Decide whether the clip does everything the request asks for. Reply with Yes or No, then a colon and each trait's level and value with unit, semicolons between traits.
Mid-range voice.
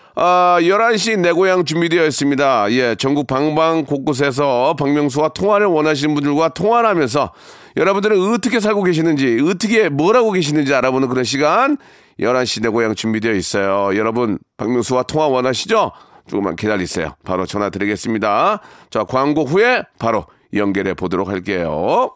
Yes: medium, 145 Hz